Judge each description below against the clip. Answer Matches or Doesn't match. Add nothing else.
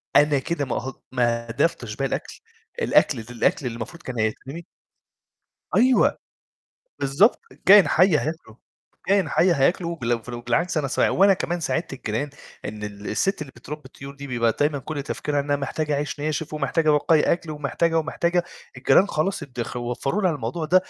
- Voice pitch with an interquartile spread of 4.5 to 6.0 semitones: Matches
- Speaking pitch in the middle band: Matches